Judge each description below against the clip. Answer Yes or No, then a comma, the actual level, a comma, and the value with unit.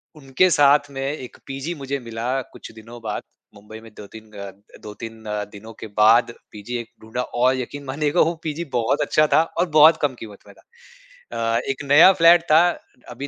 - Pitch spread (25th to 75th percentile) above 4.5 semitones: Yes, average, 5.2 semitones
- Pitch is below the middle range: Yes, low, 130 Hz